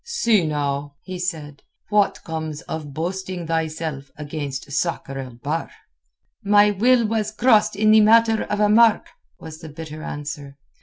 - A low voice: No, medium, 165 Hz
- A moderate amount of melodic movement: No, wide, 6.1 semitones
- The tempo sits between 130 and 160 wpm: Yes, average, 150 wpm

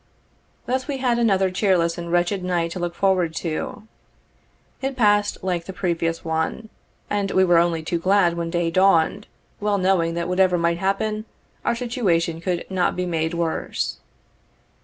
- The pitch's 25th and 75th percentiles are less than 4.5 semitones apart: Yes, average, 3.1 semitones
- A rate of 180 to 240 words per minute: No, average, 160 wpm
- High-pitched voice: No, medium, 180 Hz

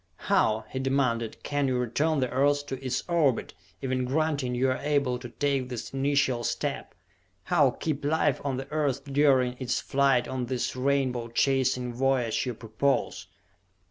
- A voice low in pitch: Yes, low, 130 Hz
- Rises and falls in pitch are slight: Yes, narrow, 2.2 semitones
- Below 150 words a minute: No, average, 160 wpm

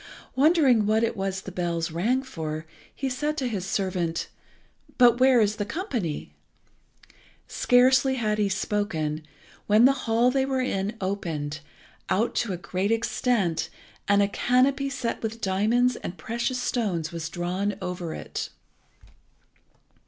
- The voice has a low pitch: No, high, 210 Hz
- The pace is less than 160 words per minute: Yes, average, 140 wpm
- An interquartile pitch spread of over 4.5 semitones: Yes, wide, 5.4 semitones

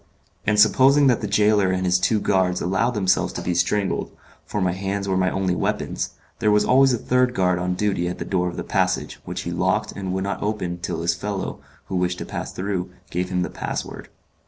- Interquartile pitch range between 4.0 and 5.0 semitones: No, narrow, 2.6 semitones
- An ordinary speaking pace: No, fast, 225 wpm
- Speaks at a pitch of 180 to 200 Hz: No, very low, 95 Hz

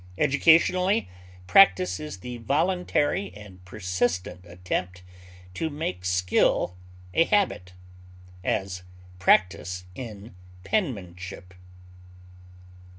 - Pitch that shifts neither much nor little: No, wide, 9.0 semitones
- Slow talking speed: Yes, slow, 80 wpm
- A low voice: Yes, low, 100 Hz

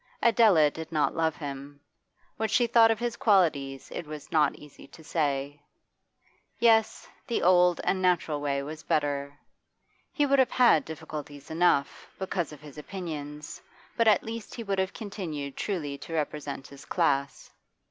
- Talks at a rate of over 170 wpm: No, average, 160 wpm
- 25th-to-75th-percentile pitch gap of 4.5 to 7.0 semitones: Yes, wide, 5.6 semitones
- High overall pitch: No, medium, 160 Hz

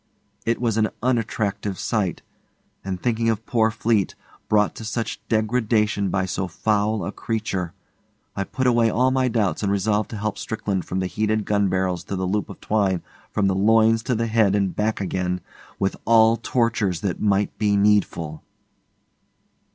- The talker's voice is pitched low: Yes, low, 105 Hz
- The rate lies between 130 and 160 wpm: No, average, 170 wpm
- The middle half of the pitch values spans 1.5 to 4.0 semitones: Yes, narrow, 2.6 semitones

